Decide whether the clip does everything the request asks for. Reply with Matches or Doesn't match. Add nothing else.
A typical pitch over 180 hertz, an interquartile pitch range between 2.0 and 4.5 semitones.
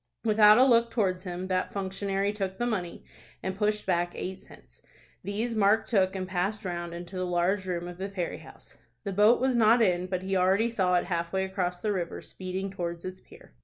Matches